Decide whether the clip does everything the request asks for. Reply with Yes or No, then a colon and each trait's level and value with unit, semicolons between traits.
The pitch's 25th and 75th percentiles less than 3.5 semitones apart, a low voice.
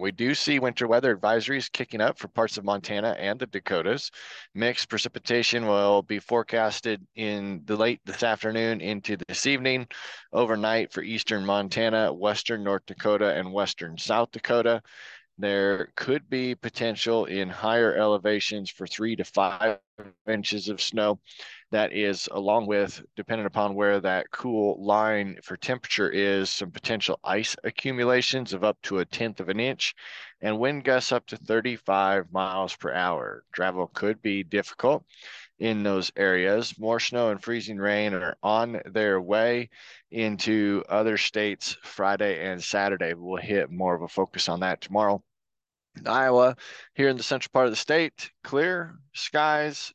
Yes: average, 2.9 semitones; low, 110 Hz